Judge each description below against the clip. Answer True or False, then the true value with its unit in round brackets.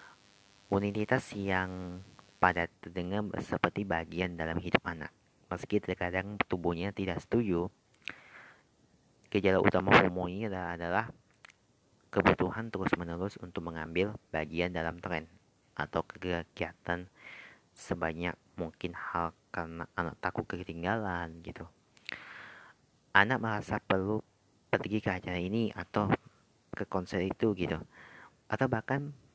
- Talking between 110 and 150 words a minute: False (100 wpm)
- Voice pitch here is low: True (95 Hz)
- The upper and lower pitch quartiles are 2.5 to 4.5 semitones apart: True (3.2 semitones)